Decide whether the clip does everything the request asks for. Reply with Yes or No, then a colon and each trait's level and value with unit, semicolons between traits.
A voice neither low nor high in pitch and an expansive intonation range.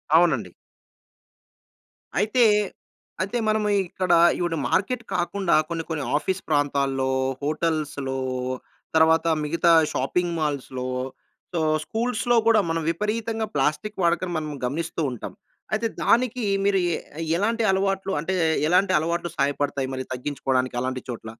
Yes: medium, 170 Hz; wide, 5.9 semitones